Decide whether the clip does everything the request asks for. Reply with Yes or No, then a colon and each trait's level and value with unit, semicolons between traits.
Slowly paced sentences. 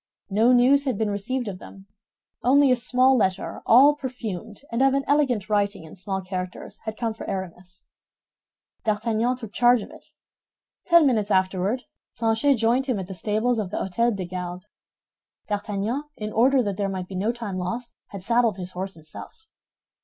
No: average, 175 wpm